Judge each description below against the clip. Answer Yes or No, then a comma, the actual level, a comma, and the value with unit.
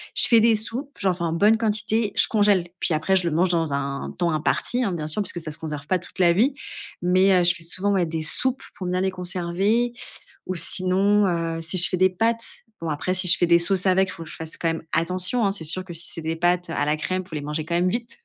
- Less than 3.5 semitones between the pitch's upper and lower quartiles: Yes, average, 3.0 semitones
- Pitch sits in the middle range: Yes, medium, 180 Hz